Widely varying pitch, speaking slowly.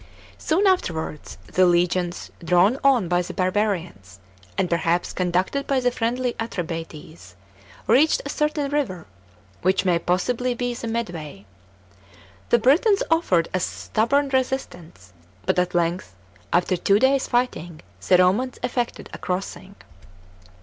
Yes: wide, 6.4 semitones; slow, 130 wpm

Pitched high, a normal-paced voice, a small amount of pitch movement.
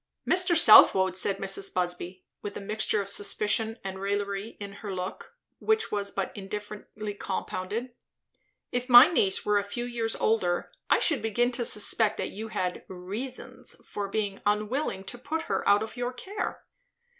No: high, 210 Hz; average, 165 wpm; average, 3.5 semitones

